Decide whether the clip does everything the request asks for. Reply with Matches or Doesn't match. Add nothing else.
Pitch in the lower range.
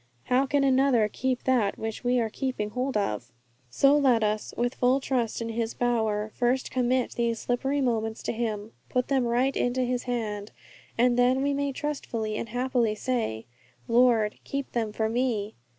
Doesn't match